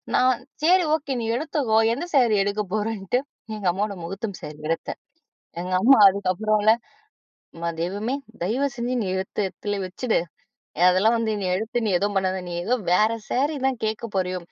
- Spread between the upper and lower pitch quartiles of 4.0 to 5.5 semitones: Yes, average, 4.5 semitones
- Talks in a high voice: Yes, high, 215 Hz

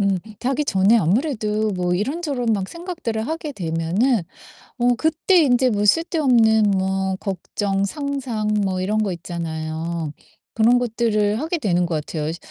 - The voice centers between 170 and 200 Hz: No, high, 215 Hz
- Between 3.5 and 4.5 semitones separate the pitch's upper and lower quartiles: No, wide, 5.5 semitones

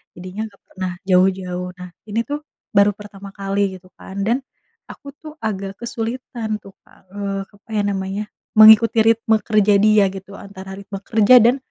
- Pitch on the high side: Yes, high, 200 Hz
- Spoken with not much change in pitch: Yes, narrow, 2.2 semitones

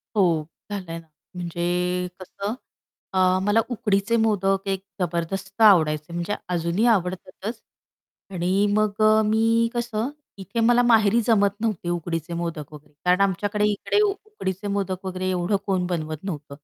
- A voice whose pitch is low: No, high, 190 Hz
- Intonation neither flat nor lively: Yes, average, 3.5 semitones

